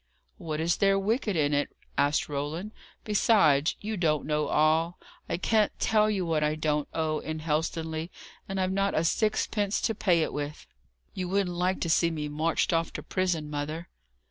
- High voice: No, medium, 165 Hz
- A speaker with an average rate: Yes, average, 180 wpm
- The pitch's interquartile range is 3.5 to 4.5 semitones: Yes, average, 4.1 semitones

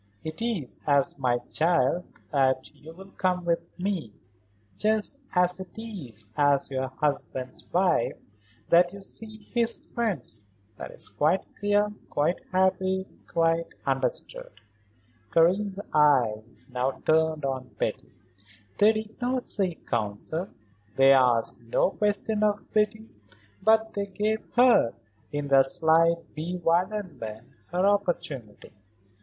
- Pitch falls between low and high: Yes, medium, 170 Hz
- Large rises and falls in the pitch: Yes, wide, 7.1 semitones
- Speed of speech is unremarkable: No, slow, 120 wpm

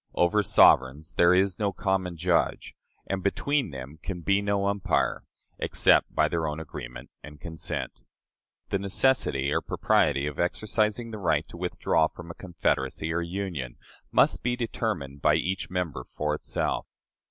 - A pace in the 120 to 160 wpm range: Yes, average, 155 wpm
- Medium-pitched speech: No, very low, 85 Hz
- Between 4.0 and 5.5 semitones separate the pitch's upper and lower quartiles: Yes, average, 4.7 semitones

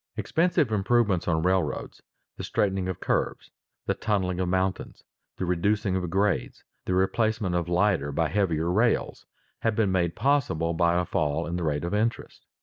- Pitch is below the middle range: Yes, very low, 95 Hz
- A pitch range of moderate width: Yes, average, 3.4 semitones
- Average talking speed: Yes, average, 165 wpm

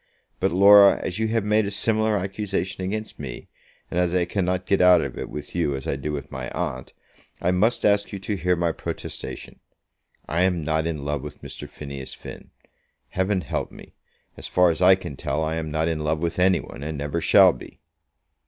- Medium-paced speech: No, fast, 210 wpm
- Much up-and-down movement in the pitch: No, average, 4.2 semitones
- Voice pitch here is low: Yes, very low, 90 Hz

